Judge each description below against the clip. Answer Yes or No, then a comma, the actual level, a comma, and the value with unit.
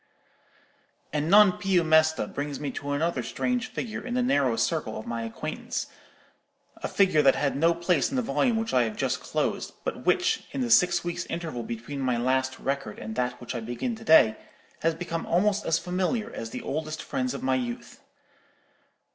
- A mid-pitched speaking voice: Yes, medium, 150 Hz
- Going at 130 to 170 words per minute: No, average, 190 wpm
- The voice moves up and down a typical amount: No, wide, 6.0 semitones